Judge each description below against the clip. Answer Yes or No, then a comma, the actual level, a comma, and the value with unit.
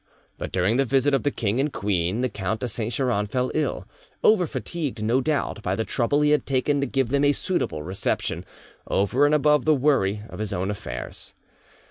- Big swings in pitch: Yes, wide, 5.7 semitones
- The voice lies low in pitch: Yes, low, 125 Hz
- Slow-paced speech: No, fast, 205 wpm